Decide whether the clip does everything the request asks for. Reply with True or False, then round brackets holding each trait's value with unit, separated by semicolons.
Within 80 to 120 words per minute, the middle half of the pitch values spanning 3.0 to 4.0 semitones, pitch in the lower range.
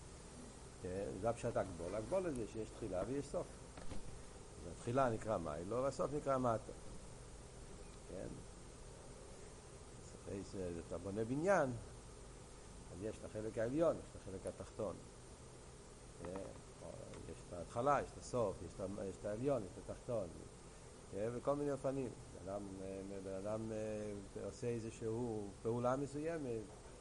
True (115 wpm; 3.6 semitones; 110 Hz)